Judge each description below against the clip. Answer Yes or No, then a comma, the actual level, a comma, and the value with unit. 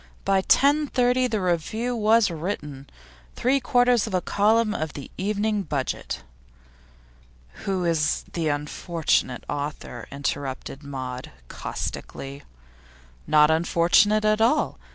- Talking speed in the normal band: No, slow, 110 wpm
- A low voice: No, medium, 180 Hz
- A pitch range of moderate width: No, wide, 6.8 semitones